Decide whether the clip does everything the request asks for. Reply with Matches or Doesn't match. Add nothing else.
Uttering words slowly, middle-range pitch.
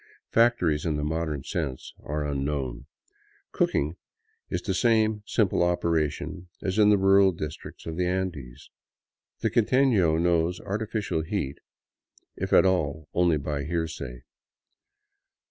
Doesn't match